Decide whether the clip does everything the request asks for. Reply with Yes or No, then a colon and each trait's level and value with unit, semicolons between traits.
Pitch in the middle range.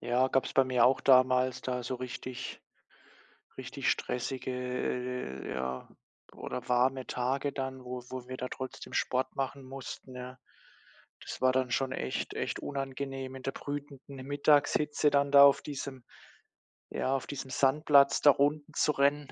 No: low, 130 Hz